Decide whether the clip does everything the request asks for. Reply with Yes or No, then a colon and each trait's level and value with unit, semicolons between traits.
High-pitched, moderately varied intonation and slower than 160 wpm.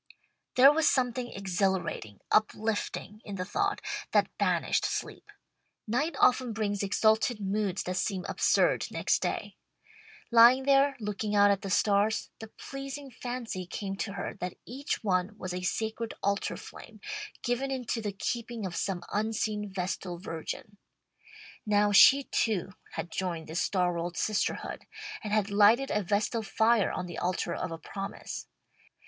Yes: high, 210 Hz; average, 3.6 semitones; average, 150 wpm